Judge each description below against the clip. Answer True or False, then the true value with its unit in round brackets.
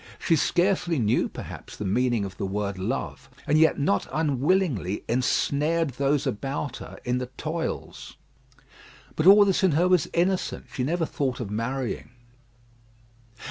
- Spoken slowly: False (145 wpm)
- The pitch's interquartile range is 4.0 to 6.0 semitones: True (5.5 semitones)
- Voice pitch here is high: False (140 Hz)